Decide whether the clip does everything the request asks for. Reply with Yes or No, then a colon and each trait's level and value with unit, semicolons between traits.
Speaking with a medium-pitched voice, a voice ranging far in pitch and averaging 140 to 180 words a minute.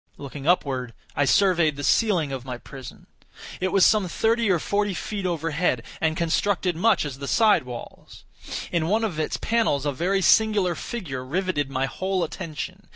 Yes: medium, 170 Hz; wide, 5.7 semitones; average, 170 wpm